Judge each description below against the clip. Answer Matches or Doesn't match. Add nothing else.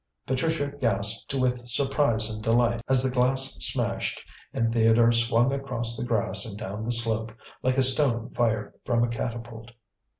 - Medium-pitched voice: Doesn't match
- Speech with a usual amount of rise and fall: Doesn't match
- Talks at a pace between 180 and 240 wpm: Doesn't match